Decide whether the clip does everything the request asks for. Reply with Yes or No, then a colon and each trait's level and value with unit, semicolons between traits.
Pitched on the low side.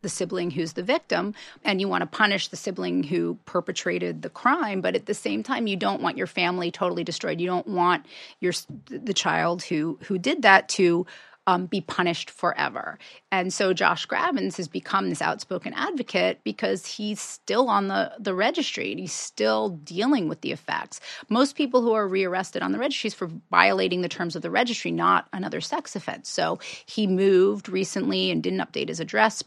No: medium, 185 Hz